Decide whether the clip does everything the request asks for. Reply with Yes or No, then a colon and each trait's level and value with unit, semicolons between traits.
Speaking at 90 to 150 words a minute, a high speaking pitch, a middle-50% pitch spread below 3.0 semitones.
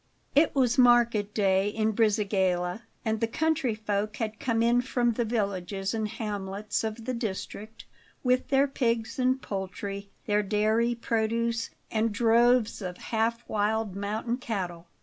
Yes: average, 145 wpm; high, 220 Hz; narrow, 2.5 semitones